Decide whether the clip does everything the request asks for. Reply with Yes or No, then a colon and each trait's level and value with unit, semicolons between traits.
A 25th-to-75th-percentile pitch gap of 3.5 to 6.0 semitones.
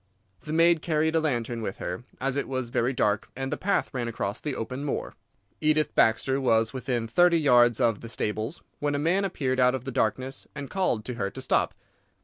Yes: average, 4.5 semitones